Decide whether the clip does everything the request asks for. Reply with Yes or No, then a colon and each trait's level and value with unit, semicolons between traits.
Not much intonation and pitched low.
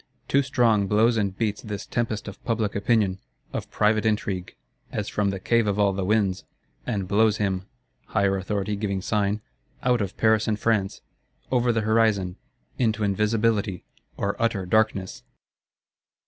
Yes: narrow, 2.1 semitones; low, 105 Hz